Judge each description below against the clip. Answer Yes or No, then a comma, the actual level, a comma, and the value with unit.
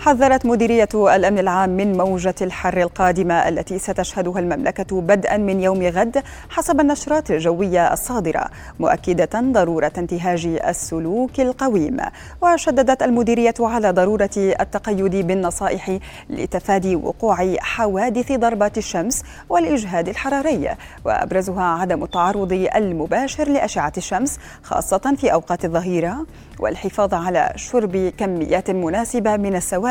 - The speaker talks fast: No, average, 110 wpm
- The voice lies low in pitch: No, high, 195 Hz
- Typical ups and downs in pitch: Yes, average, 4.5 semitones